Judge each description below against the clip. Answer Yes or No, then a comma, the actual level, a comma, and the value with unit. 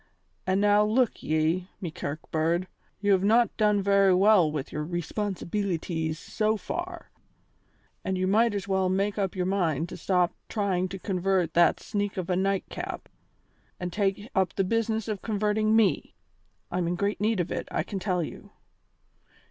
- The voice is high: Yes, high, 195 Hz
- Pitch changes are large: No, average, 2.8 semitones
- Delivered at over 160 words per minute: Yes, average, 170 wpm